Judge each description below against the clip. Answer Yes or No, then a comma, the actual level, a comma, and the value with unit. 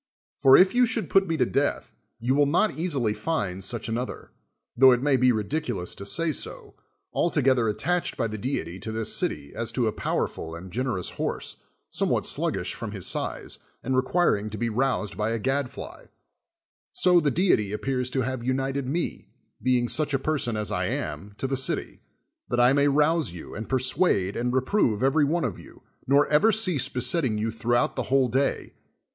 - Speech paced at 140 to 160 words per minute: No, average, 195 wpm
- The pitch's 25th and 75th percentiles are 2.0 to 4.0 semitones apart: No, average, 4.7 semitones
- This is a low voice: Yes, low, 130 Hz